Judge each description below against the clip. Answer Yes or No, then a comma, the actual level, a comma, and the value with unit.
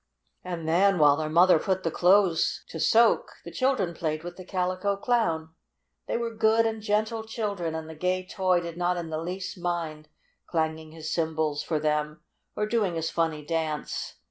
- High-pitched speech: No, medium, 175 Hz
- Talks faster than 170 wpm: Yes, average, 180 wpm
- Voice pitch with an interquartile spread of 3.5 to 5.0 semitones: Yes, average, 3.8 semitones